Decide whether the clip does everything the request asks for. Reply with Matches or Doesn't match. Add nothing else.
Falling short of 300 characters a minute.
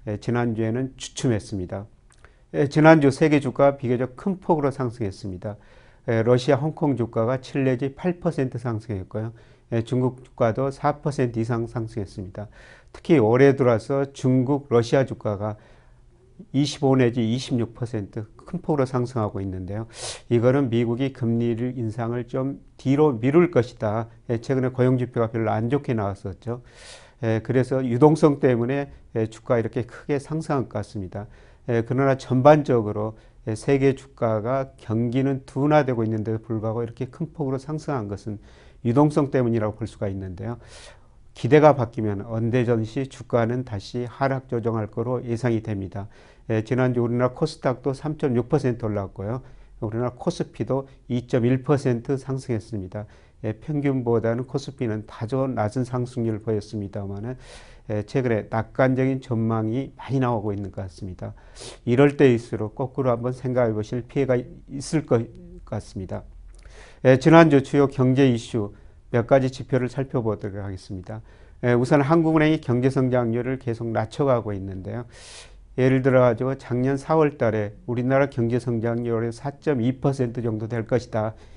Doesn't match